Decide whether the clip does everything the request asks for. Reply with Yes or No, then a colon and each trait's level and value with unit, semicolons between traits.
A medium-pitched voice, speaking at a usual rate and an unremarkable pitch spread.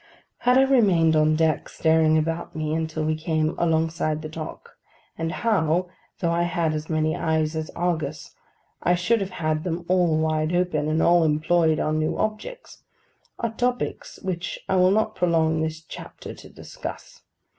No: medium, 160 Hz; average, 165 wpm; narrow, 2.2 semitones